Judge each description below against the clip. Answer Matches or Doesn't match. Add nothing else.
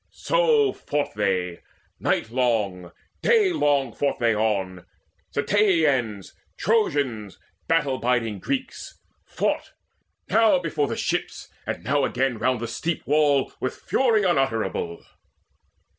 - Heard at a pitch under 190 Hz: Matches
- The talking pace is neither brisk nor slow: Doesn't match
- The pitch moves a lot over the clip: Matches